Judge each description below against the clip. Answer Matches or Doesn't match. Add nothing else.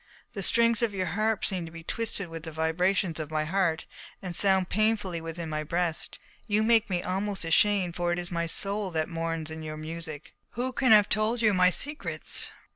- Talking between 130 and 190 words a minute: Doesn't match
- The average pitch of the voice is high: Doesn't match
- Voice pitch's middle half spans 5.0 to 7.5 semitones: Doesn't match